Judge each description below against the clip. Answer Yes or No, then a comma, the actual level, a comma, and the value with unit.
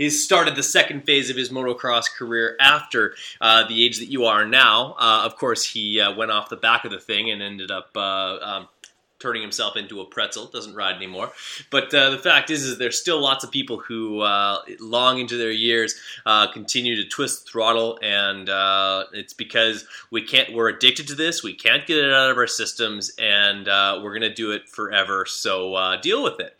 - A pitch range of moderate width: Yes, average, 4.1 semitones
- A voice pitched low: Yes, low, 115 Hz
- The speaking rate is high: Yes, fast, 215 wpm